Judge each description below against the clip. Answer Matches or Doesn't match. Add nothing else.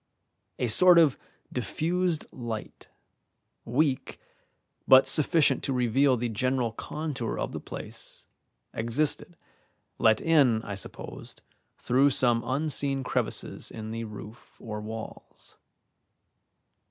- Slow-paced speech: Matches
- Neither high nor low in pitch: Doesn't match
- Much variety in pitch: Doesn't match